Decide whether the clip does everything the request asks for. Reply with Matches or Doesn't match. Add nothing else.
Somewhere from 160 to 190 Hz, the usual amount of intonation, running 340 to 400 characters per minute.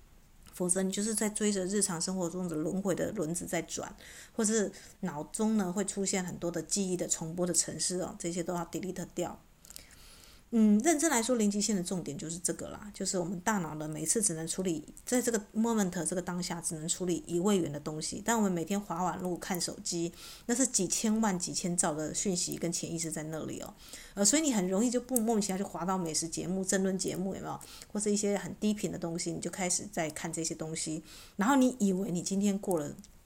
Matches